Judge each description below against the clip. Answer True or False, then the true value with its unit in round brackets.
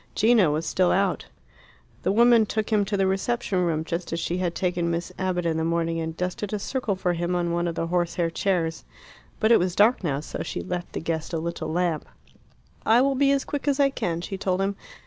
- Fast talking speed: True (230 wpm)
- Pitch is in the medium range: True (180 Hz)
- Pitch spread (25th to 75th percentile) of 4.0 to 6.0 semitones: False (3.4 semitones)